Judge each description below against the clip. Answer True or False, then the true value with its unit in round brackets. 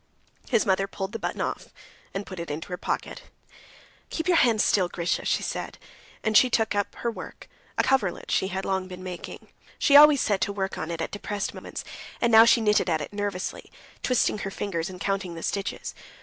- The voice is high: True (200 Hz)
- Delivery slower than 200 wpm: False (205 wpm)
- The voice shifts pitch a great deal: False (3.2 semitones)